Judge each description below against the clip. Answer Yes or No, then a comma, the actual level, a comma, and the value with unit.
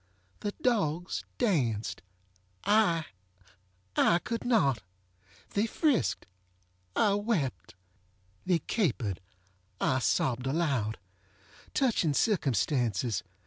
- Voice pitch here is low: Yes, low, 130 Hz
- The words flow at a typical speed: No, slow, 65 wpm